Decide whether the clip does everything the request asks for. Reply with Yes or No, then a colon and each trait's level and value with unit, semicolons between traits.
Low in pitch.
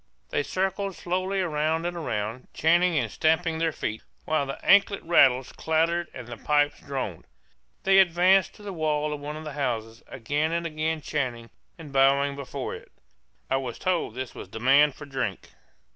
No: medium, 150 Hz